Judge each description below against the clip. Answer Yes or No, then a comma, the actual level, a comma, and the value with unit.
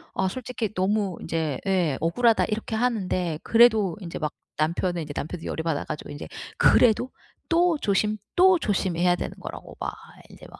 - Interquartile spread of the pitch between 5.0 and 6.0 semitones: Yes, average, 5.3 semitones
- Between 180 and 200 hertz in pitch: Yes, high, 190 Hz